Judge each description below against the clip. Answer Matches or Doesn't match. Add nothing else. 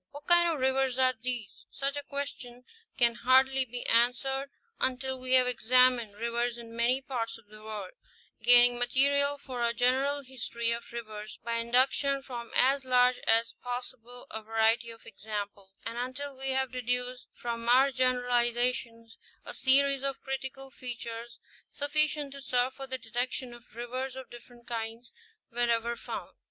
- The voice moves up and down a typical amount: Doesn't match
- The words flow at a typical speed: Matches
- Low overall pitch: Doesn't match